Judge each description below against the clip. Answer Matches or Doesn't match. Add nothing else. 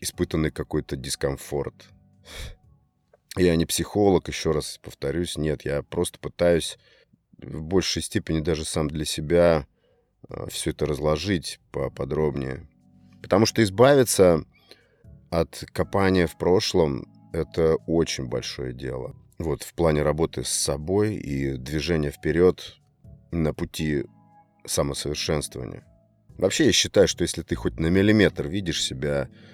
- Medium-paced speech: Matches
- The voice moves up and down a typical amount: Matches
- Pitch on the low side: Matches